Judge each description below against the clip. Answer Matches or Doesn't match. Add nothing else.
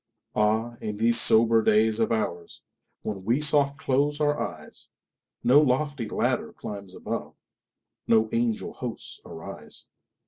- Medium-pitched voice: Doesn't match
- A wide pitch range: Doesn't match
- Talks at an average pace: Doesn't match